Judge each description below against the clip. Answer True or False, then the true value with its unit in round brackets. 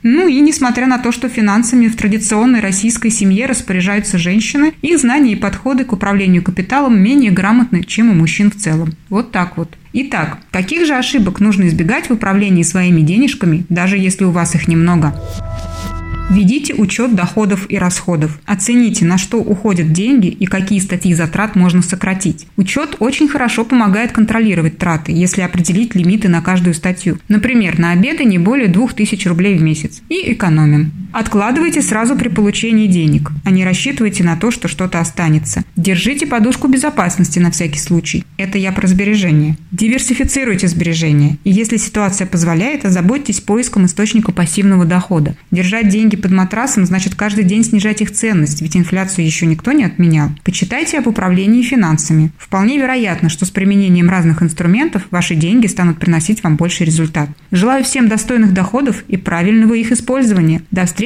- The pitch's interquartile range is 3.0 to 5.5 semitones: True (4.4 semitones)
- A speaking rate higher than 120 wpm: True (160 wpm)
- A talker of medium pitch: False (195 Hz)